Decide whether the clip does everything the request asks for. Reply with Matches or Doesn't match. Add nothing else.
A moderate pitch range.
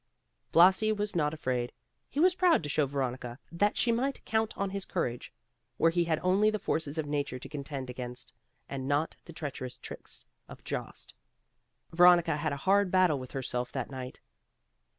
Doesn't match